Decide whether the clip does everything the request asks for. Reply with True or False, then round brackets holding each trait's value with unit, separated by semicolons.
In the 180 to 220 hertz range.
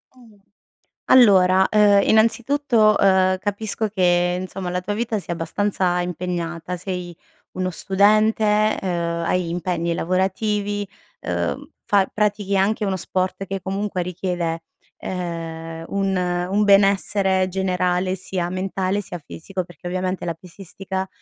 True (190 Hz)